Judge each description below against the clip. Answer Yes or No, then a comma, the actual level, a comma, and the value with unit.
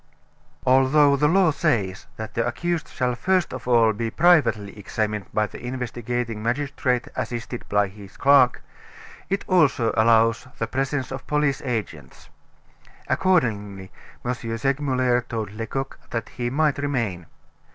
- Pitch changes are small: No, average, 4.0 semitones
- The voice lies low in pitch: Yes, low, 125 Hz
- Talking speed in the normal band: No, slow, 130 wpm